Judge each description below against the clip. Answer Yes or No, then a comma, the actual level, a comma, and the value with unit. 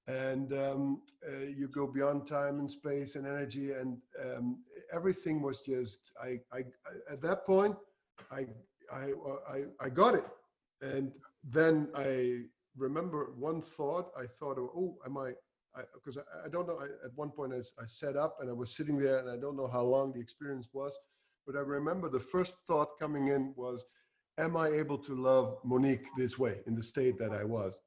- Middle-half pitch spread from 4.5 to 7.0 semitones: No, narrow, 2.5 semitones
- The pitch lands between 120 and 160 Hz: Yes, medium, 140 Hz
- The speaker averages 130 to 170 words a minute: No, average, 195 wpm